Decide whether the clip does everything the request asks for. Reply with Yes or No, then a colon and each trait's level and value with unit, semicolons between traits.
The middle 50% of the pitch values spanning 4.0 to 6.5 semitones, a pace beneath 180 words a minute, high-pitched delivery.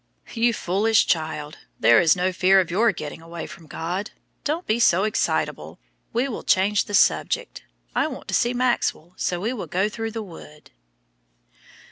Yes: average, 4.7 semitones; average, 170 wpm; high, 195 Hz